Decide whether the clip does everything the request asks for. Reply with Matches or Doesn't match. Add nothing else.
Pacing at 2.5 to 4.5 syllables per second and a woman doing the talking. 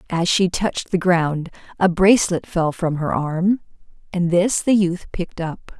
Matches